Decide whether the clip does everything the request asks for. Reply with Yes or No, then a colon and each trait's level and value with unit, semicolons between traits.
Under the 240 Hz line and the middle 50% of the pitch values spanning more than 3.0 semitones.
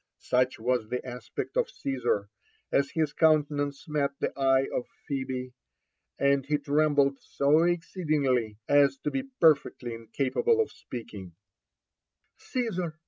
Yes: medium, 140 Hz; average, 3.4 semitones